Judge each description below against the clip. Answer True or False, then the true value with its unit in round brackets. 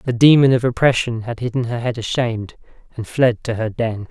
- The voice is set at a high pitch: False (120 Hz)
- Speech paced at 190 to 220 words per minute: True (205 wpm)